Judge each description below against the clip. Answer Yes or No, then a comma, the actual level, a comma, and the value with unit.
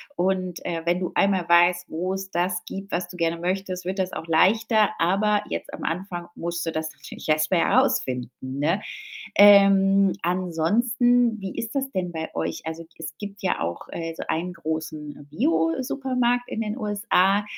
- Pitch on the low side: No, medium, 180 Hz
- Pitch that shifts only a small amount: No, average, 3.5 semitones